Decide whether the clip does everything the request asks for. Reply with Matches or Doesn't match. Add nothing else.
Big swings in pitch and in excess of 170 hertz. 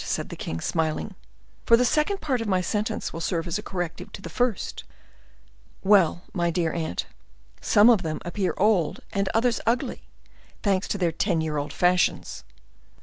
Doesn't match